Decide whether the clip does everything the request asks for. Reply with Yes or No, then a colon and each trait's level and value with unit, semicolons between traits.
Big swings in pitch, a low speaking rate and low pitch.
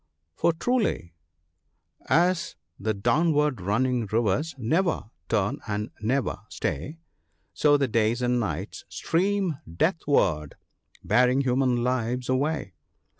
Yes: wide, 6.1 semitones; slow, 110 wpm; low, 125 Hz